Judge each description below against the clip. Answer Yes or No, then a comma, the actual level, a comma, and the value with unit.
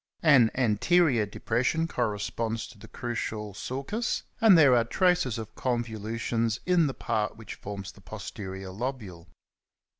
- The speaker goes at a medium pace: No, slow, 130 wpm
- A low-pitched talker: Yes, low, 115 Hz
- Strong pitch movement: No, average, 4.1 semitones